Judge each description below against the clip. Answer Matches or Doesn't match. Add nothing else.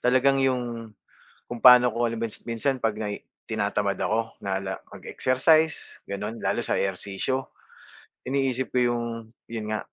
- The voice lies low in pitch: Matches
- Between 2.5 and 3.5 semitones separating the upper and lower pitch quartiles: Matches